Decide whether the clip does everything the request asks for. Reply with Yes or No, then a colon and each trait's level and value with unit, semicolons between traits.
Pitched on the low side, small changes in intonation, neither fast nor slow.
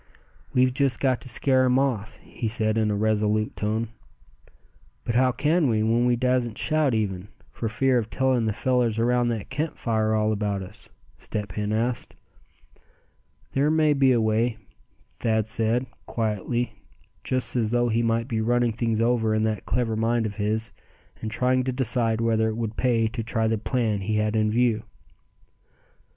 Yes: low, 115 Hz; narrow, 2.3 semitones; average, 175 wpm